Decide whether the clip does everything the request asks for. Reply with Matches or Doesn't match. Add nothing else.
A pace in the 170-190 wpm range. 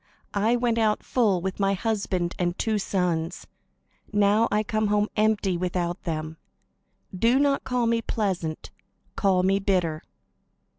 Doesn't match